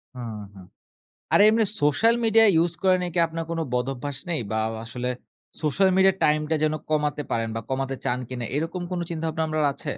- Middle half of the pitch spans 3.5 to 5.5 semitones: Yes, average, 4.8 semitones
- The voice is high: No, medium, 155 Hz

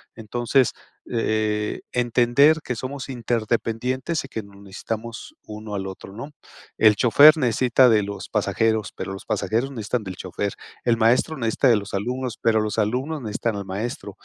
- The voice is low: Yes, low, 115 Hz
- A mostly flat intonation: No, average, 3.0 semitones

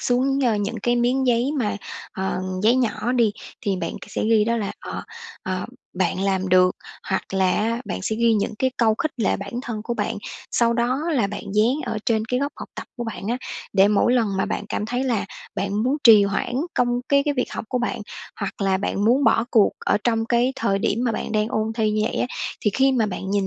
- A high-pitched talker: Yes, high, 225 Hz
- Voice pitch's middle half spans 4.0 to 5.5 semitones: No, average, 3.2 semitones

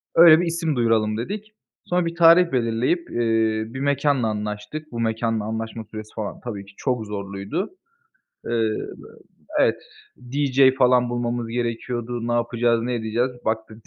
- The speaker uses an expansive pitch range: No, average, 3.5 semitones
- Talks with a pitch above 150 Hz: No, low, 120 Hz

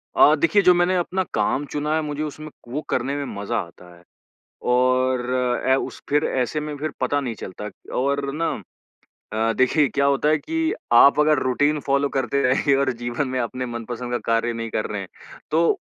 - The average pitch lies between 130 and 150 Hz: Yes, medium, 140 Hz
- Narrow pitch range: No, average, 3.6 semitones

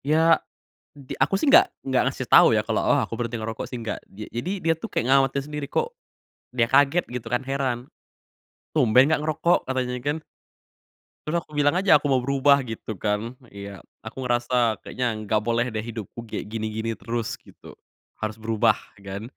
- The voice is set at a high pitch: No, low, 125 Hz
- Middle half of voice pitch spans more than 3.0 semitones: Yes, average, 4.2 semitones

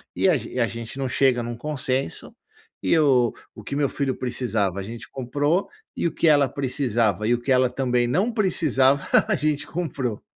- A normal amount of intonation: Yes, average, 3.4 semitones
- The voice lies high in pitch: No, low, 130 Hz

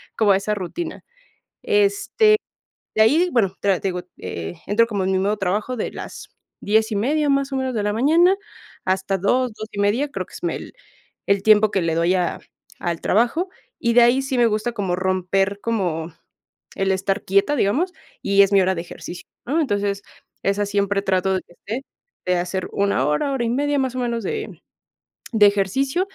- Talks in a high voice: Yes, high, 205 Hz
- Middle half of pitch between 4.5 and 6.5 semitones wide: Yes, average, 5.0 semitones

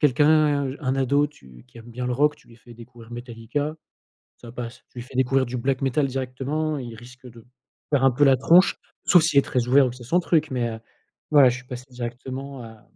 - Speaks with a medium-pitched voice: No, low, 130 Hz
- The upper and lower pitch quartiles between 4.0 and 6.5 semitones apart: No, average, 2.9 semitones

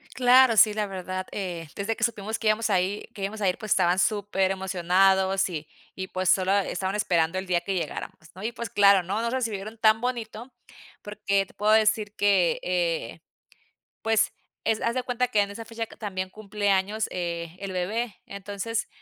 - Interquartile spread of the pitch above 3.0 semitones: No, average, 2.7 semitones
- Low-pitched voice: No, high, 200 Hz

